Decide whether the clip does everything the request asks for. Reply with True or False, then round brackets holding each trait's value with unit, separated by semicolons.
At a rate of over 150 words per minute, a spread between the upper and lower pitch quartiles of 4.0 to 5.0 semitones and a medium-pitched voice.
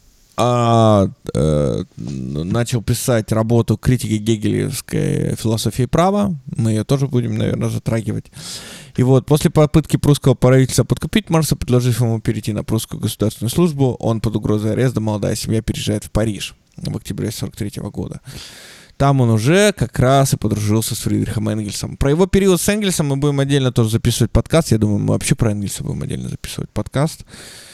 False (160 wpm; 4.5 semitones; 120 Hz)